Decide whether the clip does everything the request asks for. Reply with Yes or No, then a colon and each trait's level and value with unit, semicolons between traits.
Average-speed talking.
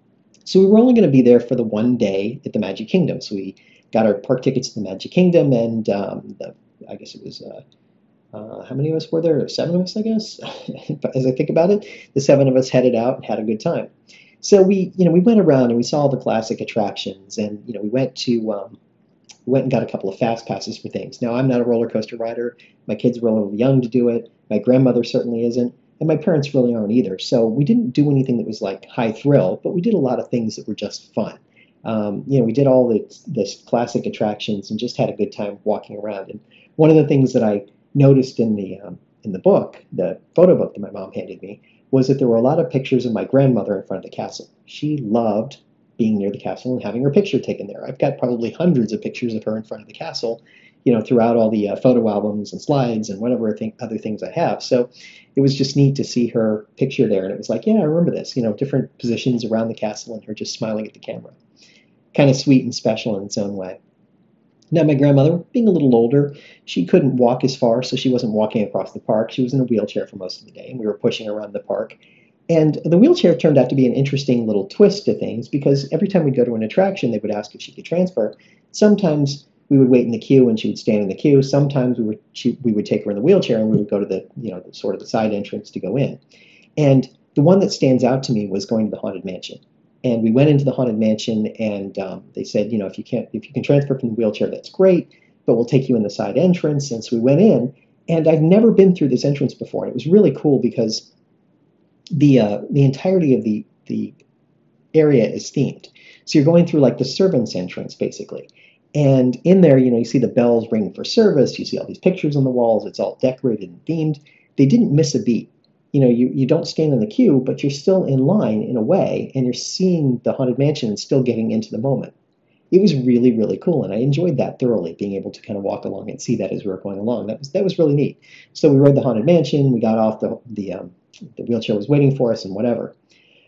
No: fast, 260 wpm